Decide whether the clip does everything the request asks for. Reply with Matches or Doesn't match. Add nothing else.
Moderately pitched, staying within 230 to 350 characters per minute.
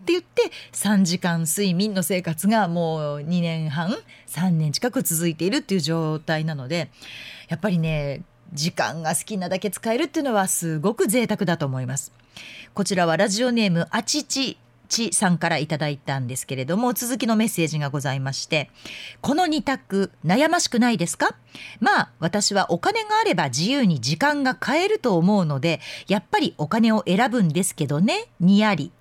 Matches